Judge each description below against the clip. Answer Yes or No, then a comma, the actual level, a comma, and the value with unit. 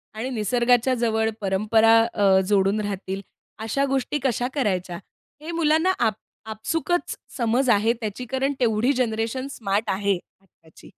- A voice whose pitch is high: Yes, high, 225 Hz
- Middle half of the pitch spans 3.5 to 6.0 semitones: Yes, average, 4.0 semitones